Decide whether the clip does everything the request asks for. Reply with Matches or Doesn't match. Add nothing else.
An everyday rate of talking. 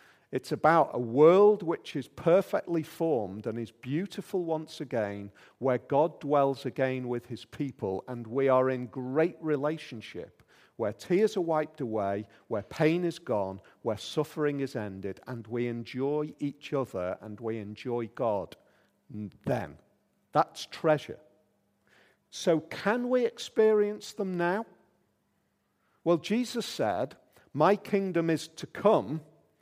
Doesn't match